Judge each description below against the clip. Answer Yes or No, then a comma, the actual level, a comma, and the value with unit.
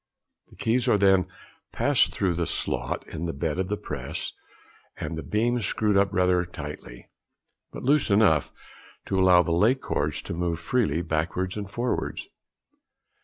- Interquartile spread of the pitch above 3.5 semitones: Yes, average, 4.1 semitones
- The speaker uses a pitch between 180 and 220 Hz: No, very low, 90 Hz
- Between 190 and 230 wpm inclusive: No, average, 165 wpm